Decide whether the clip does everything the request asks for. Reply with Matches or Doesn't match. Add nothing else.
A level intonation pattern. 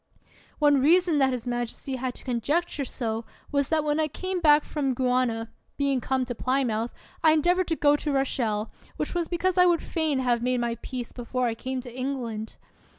Doesn't match